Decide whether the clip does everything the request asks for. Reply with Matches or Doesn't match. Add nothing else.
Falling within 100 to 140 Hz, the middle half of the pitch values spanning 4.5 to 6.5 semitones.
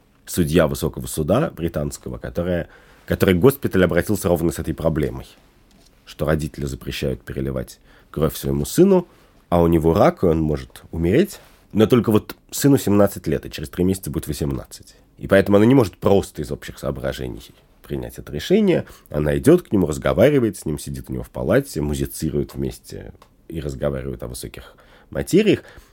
Doesn't match